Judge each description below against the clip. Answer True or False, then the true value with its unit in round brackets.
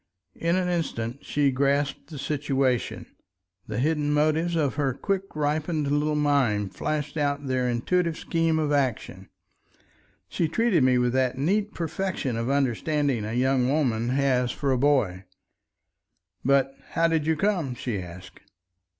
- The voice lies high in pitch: False (140 Hz)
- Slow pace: False (145 wpm)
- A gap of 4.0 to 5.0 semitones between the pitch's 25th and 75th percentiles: False (3.6 semitones)